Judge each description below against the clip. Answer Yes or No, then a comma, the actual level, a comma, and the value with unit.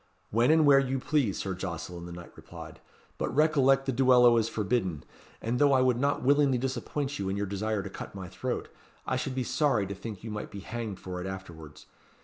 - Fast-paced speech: Yes, fast, 215 wpm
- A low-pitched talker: Yes, low, 115 Hz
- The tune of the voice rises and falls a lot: Yes, wide, 5.8 semitones